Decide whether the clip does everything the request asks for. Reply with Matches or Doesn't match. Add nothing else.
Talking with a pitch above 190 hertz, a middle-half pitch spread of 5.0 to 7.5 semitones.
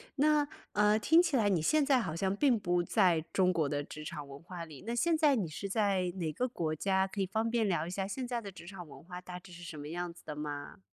Doesn't match